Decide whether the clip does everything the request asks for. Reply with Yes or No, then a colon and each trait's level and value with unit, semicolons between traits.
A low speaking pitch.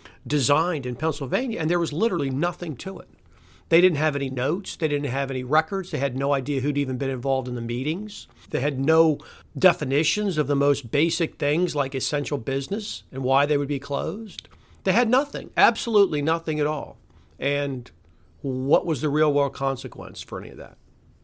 No: medium, 145 Hz